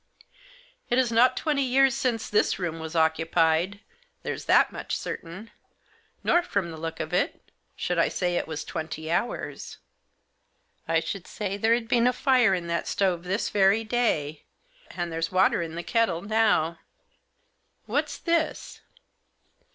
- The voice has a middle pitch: No, high, 195 Hz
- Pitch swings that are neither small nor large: No, wide, 6.5 semitones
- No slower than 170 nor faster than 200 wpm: No, average, 155 wpm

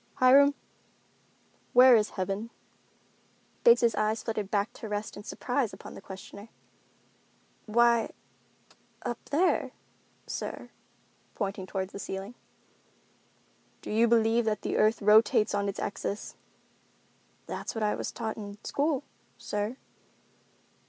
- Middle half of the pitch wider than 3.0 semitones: No, narrow, 2.6 semitones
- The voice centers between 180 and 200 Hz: No, high, 220 Hz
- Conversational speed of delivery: No, slow, 120 wpm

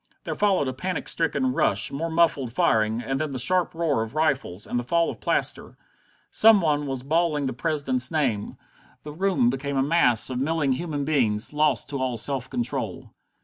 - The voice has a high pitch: No, medium, 140 Hz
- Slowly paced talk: No, average, 190 wpm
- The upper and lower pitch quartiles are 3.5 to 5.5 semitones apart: Yes, average, 4.2 semitones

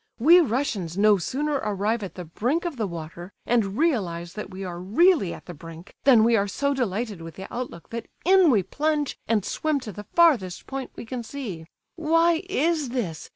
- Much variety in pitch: Yes, wide, 7.4 semitones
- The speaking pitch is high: Yes, high, 225 Hz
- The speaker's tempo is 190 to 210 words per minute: Yes, average, 200 wpm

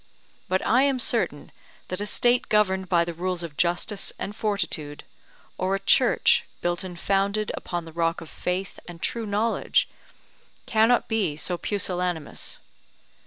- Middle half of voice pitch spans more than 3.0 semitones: Yes, average, 3.5 semitones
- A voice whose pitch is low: No, medium, 185 Hz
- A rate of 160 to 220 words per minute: No, average, 150 wpm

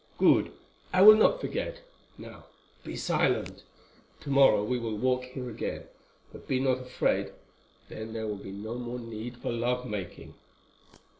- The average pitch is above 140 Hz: No, low, 125 Hz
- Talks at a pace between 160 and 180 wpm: No, average, 150 wpm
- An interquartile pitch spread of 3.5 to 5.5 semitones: No, average, 2.7 semitones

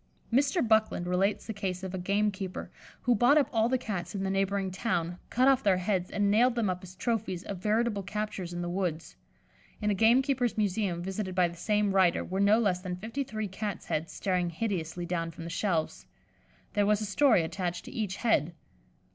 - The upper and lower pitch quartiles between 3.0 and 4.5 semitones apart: Yes, average, 3.4 semitones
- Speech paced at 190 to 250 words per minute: Yes, fast, 205 wpm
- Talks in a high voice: Yes, high, 195 Hz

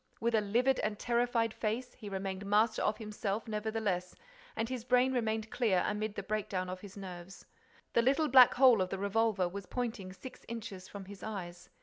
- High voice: Yes, high, 215 Hz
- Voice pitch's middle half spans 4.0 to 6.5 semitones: No, average, 3.2 semitones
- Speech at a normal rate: Yes, average, 195 wpm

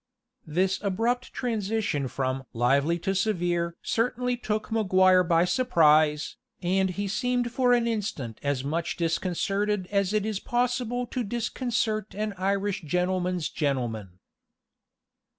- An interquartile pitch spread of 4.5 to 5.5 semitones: Yes, average, 5.1 semitones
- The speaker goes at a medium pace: No, slow, 120 wpm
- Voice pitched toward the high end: Yes, high, 195 Hz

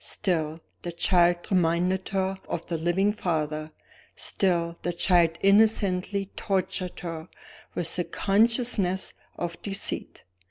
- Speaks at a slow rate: Yes, slow, 115 wpm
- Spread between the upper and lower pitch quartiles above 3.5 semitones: No, narrow, 2.6 semitones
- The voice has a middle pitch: Yes, medium, 180 Hz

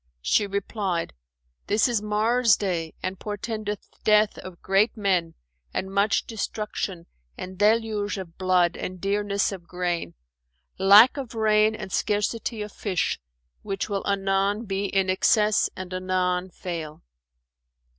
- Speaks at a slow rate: Yes, slow, 130 wpm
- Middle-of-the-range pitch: No, high, 200 Hz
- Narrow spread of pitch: Yes, narrow, 2.3 semitones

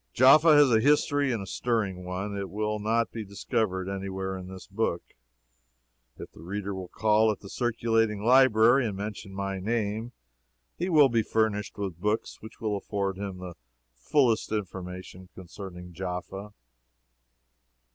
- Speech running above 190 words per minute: No, average, 155 wpm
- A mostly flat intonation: No, average, 3.0 semitones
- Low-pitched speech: Yes, low, 105 Hz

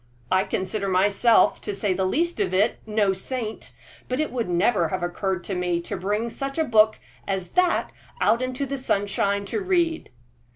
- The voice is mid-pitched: No, high, 210 Hz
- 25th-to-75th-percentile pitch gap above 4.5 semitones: Yes, average, 5.1 semitones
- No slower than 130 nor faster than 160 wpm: No, average, 180 wpm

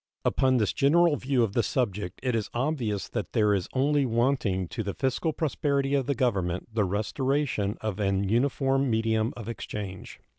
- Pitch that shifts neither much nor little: Yes, average, 4.8 semitones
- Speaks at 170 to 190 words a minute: Yes, average, 175 wpm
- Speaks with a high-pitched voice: No, low, 120 Hz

